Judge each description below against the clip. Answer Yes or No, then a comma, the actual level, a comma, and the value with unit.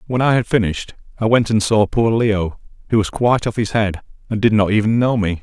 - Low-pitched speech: Yes, low, 110 Hz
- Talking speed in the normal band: No, fast, 245 wpm